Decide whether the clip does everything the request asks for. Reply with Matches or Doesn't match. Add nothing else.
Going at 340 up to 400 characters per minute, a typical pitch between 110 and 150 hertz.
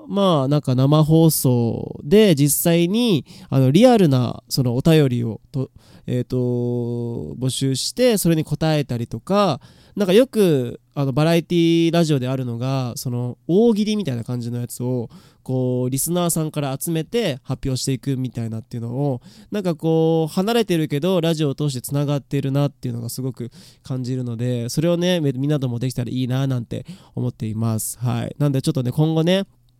Matches